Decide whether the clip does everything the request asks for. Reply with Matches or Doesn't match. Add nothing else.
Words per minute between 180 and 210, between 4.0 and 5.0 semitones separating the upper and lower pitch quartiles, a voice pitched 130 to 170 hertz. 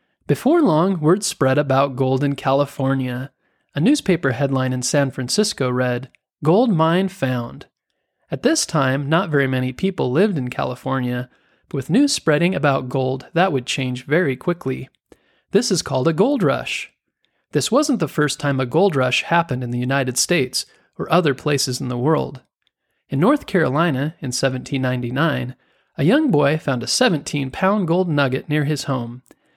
Doesn't match